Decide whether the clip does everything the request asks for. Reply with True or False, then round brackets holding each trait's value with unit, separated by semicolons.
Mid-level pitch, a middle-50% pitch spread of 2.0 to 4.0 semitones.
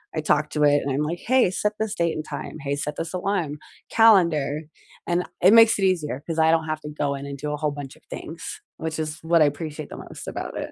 True (155 Hz; 2.9 semitones)